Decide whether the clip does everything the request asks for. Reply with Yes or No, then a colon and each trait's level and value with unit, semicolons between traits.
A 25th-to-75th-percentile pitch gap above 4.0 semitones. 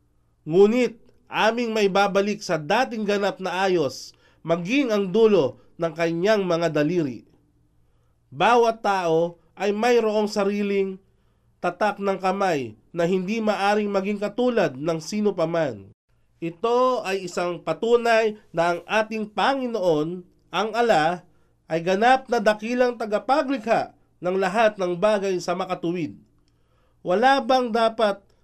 Yes: average, 4.6 semitones